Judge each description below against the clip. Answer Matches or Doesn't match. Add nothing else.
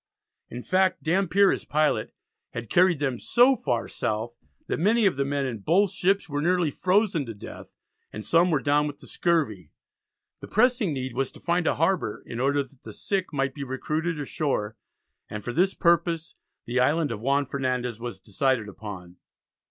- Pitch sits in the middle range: Matches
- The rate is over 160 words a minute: Matches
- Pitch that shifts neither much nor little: Doesn't match